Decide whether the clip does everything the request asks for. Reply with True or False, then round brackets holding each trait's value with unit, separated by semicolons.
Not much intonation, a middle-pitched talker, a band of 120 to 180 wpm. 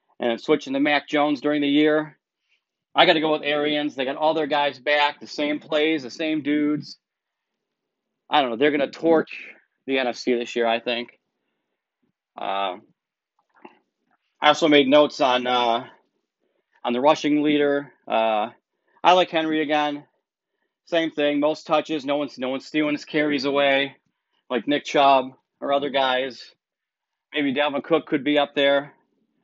True (1.9 semitones; 145 Hz; 160 wpm)